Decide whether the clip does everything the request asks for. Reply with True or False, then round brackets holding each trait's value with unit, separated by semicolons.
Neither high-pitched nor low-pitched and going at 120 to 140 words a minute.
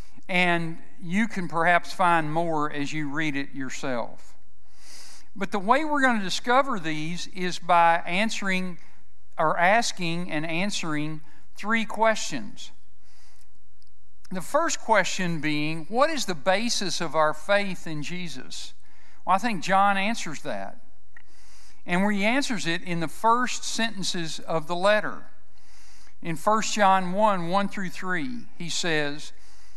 True (175 Hz; 135 wpm)